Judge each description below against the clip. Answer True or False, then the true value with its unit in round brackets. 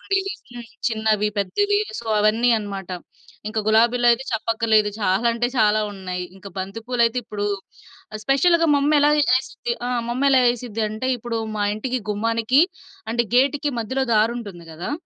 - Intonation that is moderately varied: True (3.4 semitones)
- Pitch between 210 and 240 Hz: True (230 Hz)